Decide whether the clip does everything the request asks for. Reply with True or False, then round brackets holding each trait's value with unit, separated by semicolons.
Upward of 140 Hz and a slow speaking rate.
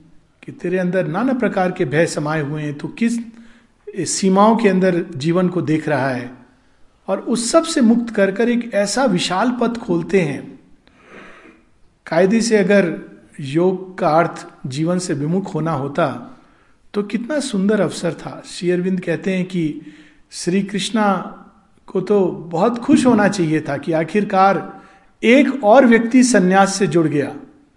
False (185 Hz; 155 wpm)